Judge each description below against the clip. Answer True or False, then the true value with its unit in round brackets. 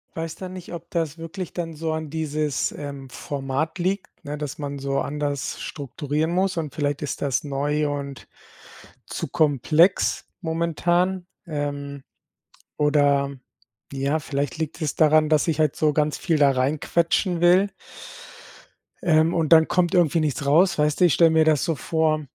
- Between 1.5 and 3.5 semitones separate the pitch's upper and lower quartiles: True (2.5 semitones)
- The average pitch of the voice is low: False (155 Hz)